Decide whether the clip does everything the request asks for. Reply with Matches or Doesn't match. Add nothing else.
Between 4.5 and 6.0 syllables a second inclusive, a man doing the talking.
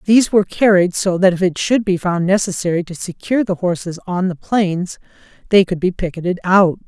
Doesn't match